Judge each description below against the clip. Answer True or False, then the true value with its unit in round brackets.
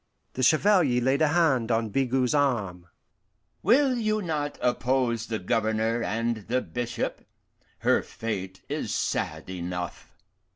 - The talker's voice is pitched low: True (120 Hz)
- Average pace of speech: False (125 wpm)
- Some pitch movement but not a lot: True (4.7 semitones)